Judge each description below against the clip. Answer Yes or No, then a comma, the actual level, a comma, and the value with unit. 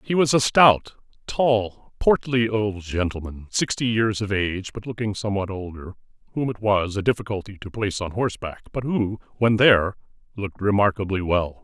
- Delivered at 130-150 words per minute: No, average, 165 wpm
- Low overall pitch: Yes, low, 105 Hz